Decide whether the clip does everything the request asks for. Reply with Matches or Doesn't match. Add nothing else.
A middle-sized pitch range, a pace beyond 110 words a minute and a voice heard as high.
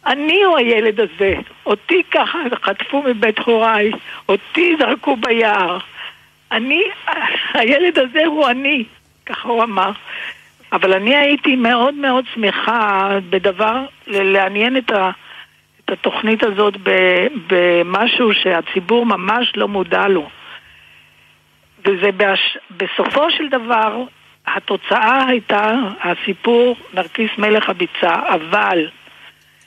Doesn't match